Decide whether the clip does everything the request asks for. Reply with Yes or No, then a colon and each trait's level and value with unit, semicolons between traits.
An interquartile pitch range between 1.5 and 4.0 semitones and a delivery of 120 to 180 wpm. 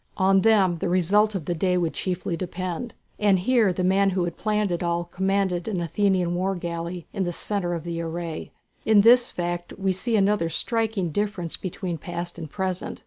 No: narrow, 2.5 semitones; average, 195 wpm